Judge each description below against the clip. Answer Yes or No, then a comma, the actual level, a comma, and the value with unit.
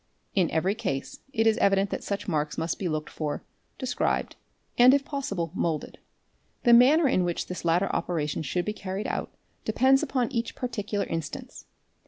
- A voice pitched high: Yes, high, 200 Hz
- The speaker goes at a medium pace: Yes, average, 170 wpm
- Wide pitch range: Yes, wide, 6.4 semitones